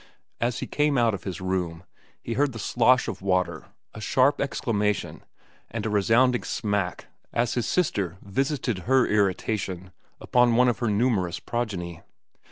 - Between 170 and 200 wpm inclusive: No, average, 155 wpm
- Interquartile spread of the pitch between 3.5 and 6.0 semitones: Yes, average, 4.6 semitones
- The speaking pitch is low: Yes, low, 110 Hz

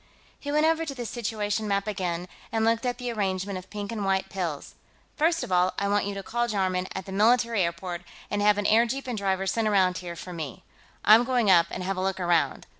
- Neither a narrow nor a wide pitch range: Yes, average, 3.7 semitones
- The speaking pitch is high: Yes, high, 200 Hz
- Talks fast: Yes, fast, 235 wpm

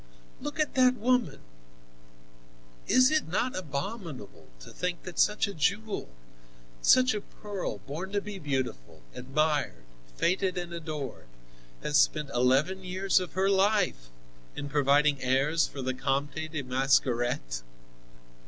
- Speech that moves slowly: Yes, slow, 130 wpm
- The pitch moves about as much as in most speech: No, wide, 6.5 semitones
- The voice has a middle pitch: Yes, medium, 155 Hz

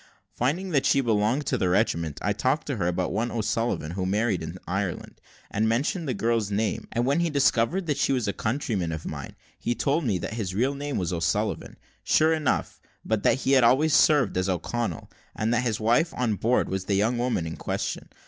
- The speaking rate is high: Yes, fast, 215 wpm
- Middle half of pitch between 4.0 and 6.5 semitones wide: Yes, wide, 5.6 semitones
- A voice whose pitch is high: No, low, 115 Hz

